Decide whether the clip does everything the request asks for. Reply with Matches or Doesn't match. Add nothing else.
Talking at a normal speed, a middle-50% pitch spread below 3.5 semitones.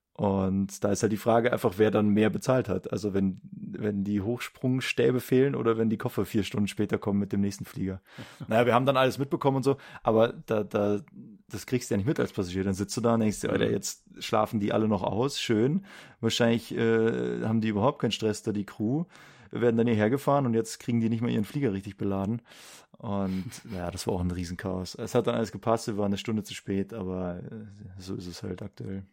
Doesn't match